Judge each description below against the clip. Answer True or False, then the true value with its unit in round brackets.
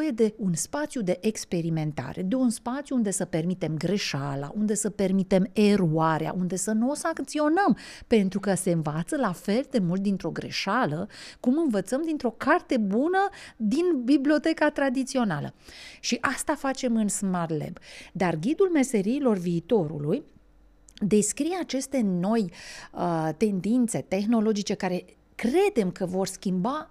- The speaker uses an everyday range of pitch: False (6.4 semitones)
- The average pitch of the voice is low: False (215 Hz)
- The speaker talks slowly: False (135 wpm)